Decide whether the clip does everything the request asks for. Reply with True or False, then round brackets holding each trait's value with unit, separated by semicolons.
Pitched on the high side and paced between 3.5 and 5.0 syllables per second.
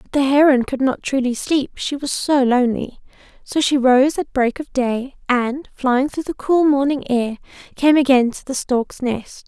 True (265 Hz; 4.4 syllables/s)